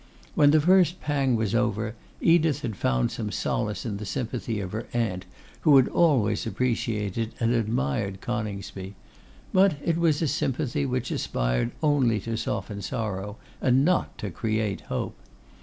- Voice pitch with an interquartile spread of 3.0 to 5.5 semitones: Yes, average, 5.1 semitones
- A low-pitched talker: Yes, low, 115 Hz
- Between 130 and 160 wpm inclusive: Yes, average, 155 wpm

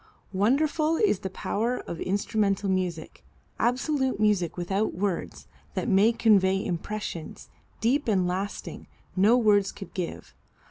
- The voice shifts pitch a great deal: No, average, 3.7 semitones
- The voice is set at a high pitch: Yes, high, 205 Hz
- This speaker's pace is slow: Yes, slow, 125 wpm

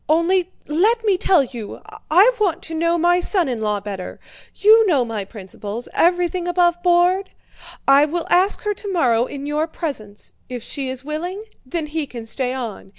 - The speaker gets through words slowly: No, average, 165 wpm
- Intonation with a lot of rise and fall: Yes, wide, 6.3 semitones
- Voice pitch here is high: Yes, very high, 320 Hz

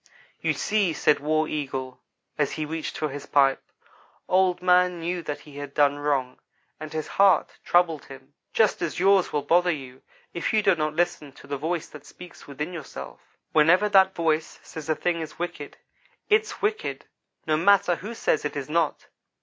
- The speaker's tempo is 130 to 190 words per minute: Yes, average, 180 wpm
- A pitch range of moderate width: Yes, average, 3.6 semitones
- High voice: No, medium, 160 Hz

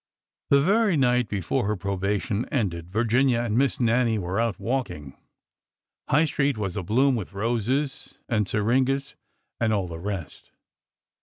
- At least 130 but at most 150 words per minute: Yes, average, 140 wpm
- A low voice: Yes, low, 115 Hz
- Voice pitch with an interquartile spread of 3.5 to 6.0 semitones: Yes, average, 5.0 semitones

